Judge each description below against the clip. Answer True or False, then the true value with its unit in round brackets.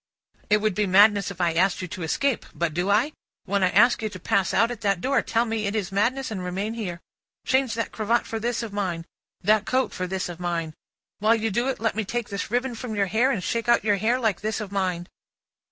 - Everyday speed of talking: False (250 wpm)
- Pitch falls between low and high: False (210 Hz)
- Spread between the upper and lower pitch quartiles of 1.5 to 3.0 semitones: False (3.6 semitones)